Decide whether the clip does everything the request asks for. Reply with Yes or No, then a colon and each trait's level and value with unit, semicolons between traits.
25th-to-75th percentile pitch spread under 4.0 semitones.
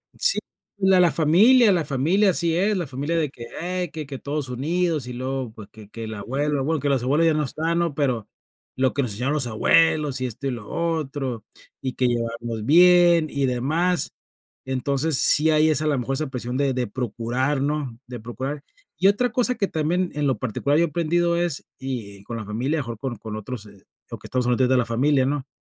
No: average, 4.7 semitones